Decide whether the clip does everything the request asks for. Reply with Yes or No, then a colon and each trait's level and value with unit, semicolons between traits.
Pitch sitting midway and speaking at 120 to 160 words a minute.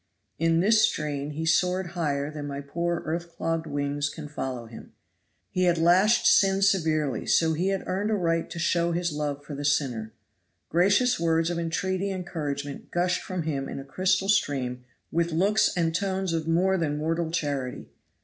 No: medium, 165 Hz; average, 180 wpm